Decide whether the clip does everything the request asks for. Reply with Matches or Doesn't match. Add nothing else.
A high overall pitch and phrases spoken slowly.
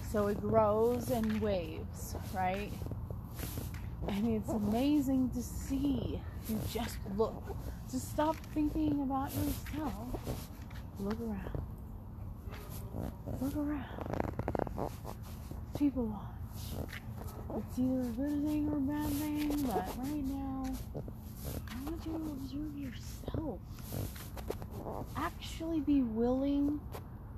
Matches